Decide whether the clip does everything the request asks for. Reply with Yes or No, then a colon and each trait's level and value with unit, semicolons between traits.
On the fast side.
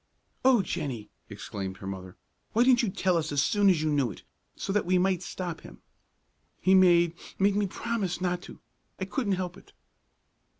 No: average, 185 wpm